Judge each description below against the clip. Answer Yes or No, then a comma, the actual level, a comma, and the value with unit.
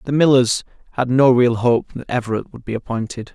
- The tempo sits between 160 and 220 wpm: Yes, average, 200 wpm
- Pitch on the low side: Yes, low, 120 Hz